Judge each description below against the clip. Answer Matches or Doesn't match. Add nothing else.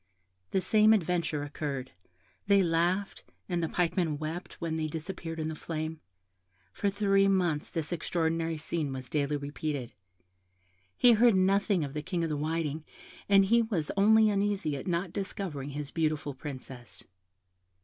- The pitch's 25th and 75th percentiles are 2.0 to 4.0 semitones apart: Doesn't match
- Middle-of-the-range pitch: Matches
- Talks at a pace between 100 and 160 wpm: Matches